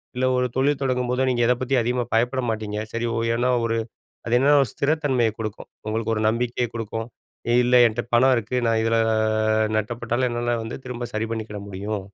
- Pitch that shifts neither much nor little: No, narrow, 2.1 semitones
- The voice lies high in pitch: No, low, 120 Hz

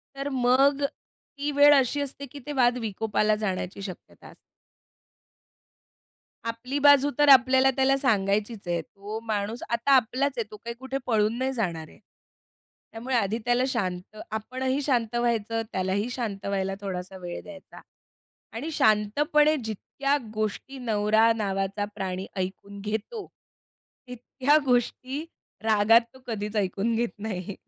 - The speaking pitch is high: Yes, high, 225 Hz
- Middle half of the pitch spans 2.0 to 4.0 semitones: No, average, 4.5 semitones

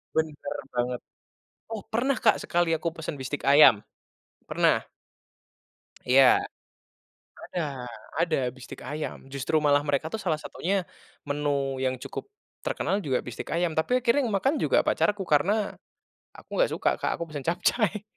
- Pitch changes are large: Yes, wide, 5.9 semitones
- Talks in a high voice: No, medium, 155 Hz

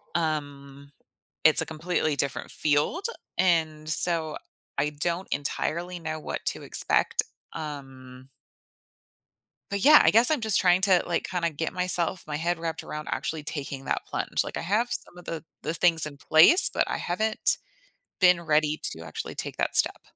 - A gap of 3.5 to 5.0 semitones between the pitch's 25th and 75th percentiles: No, average, 3.0 semitones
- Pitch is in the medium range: Yes, medium, 160 Hz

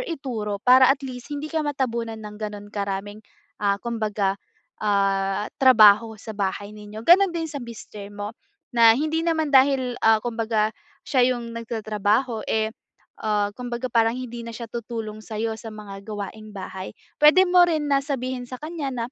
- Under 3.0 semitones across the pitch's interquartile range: No, average, 3.7 semitones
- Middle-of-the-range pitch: No, high, 230 Hz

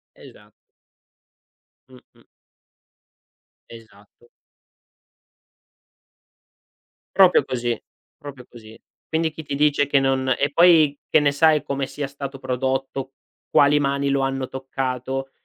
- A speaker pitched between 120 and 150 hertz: Yes, low, 135 Hz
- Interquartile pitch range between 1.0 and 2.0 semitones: Yes, narrow, 1.7 semitones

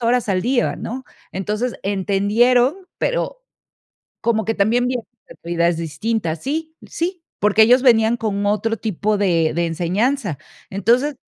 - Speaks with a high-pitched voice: Yes, high, 220 Hz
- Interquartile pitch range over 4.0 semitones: Yes, average, 4.4 semitones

